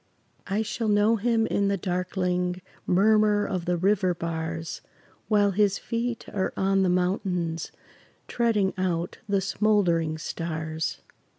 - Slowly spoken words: Yes, slow, 125 wpm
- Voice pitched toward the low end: No, high, 190 Hz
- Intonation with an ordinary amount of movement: Yes, average, 3.0 semitones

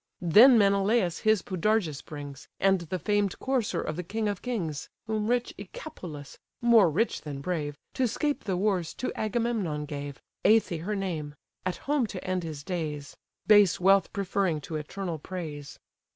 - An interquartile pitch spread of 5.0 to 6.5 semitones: Yes, wide, 5.5 semitones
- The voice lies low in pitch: No, medium, 185 Hz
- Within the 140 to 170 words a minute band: Yes, average, 160 wpm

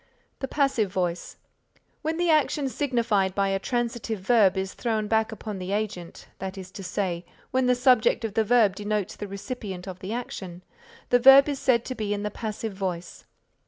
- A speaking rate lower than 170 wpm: No, average, 190 wpm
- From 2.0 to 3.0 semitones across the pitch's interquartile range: No, average, 4.3 semitones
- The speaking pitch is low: No, high, 215 Hz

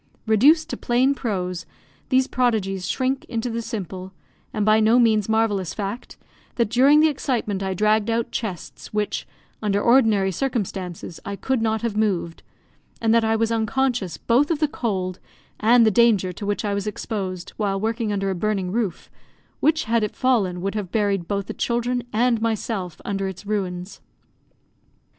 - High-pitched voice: Yes, high, 215 Hz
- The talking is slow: No, average, 170 wpm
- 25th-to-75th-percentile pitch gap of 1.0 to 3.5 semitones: Yes, average, 3.2 semitones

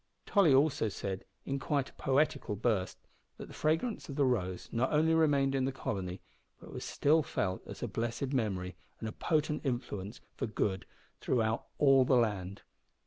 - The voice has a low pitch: Yes, low, 130 Hz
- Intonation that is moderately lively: No, wide, 5.7 semitones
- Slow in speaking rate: No, average, 175 wpm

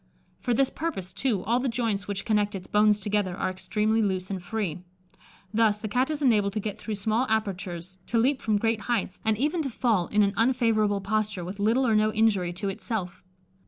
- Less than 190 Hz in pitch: No, high, 215 Hz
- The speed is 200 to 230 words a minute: Yes, fast, 205 wpm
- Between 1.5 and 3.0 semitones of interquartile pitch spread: Yes, average, 2.7 semitones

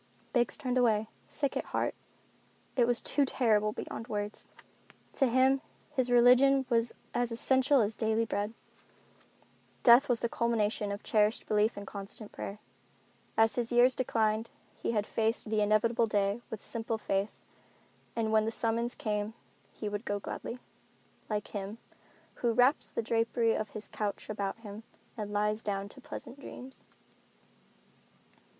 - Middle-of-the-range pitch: No, high, 225 Hz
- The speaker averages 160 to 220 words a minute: No, average, 150 wpm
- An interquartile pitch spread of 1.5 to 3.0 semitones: Yes, narrow, 2.5 semitones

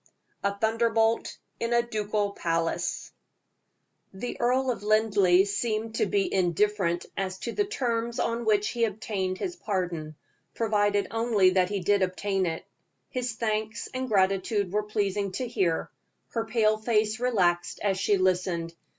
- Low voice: No, high, 210 Hz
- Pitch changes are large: No, average, 3.3 semitones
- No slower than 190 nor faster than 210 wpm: No, average, 145 wpm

